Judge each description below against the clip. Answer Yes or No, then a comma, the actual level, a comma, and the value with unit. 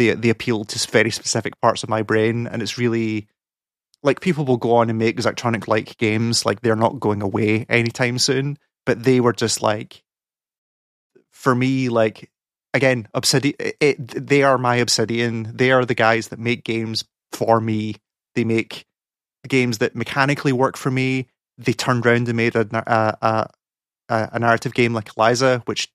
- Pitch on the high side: No, low, 120 Hz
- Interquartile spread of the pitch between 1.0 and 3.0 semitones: Yes, narrow, 2.5 semitones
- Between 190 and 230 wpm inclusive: No, average, 175 wpm